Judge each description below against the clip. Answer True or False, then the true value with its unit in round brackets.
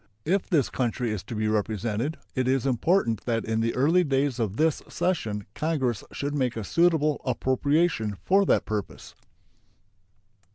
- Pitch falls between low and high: False (130 Hz)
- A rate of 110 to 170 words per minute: True (155 wpm)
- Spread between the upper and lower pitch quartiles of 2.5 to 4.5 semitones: False (5.6 semitones)